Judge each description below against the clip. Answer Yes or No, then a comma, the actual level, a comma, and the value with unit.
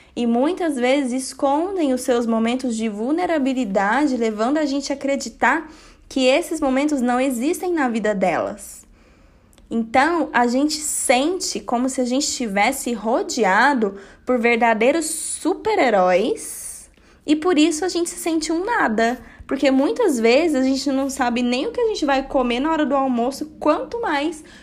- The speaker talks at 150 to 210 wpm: Yes, average, 155 wpm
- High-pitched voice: Yes, very high, 270 Hz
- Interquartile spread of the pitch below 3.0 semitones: No, average, 4.3 semitones